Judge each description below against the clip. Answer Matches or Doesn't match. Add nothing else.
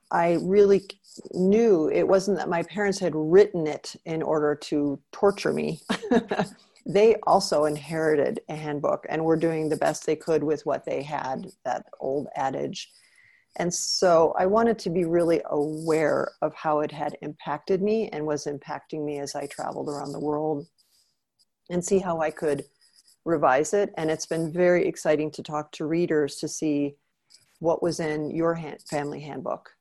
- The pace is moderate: Matches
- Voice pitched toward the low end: Doesn't match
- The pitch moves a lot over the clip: Doesn't match